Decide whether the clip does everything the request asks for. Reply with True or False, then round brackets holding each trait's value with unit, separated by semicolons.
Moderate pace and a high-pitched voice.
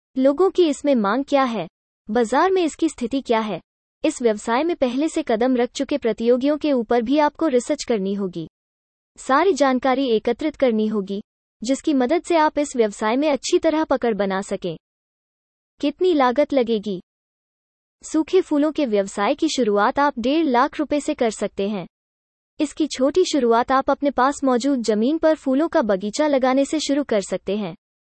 True (170 wpm; 265 Hz)